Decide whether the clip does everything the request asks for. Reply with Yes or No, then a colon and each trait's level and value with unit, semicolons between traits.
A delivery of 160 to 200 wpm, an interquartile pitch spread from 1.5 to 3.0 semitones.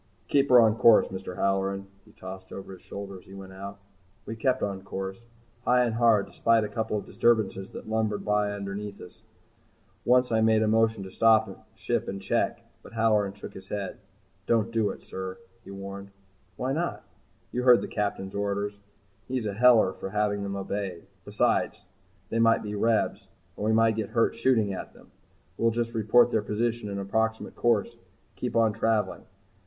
Yes: average, 185 wpm; narrow, 2.5 semitones